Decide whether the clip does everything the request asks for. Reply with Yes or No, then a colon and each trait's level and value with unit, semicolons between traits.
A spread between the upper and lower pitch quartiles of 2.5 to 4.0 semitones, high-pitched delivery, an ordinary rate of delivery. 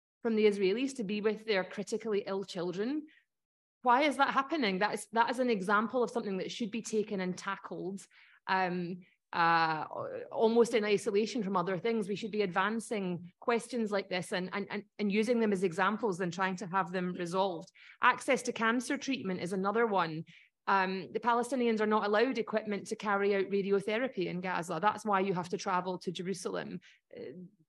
Yes: average, 3.4 semitones; high, 205 Hz; average, 185 wpm